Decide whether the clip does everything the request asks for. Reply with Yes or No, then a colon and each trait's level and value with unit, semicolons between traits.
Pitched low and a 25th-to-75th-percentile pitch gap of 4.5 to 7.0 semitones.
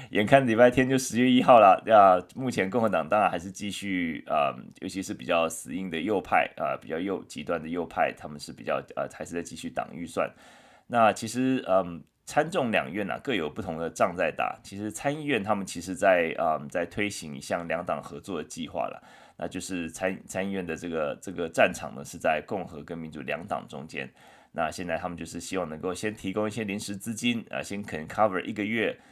No: very low, 95 Hz; average, 4.1 semitones